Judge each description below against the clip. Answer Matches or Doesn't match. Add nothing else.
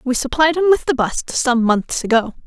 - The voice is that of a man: Doesn't match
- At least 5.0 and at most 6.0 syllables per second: Matches